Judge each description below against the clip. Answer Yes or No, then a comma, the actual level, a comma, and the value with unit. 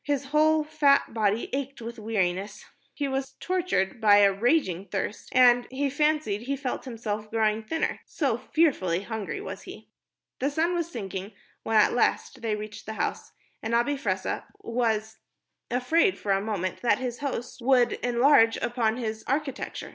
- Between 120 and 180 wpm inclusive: Yes, average, 160 wpm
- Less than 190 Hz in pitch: No, high, 240 Hz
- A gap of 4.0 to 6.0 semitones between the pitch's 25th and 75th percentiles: Yes, average, 4.6 semitones